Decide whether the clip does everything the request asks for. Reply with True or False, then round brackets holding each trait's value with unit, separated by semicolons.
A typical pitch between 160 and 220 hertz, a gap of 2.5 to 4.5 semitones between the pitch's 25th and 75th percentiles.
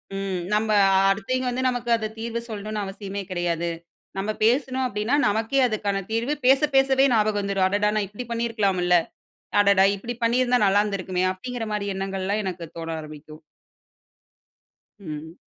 True (205 Hz; 3.5 semitones)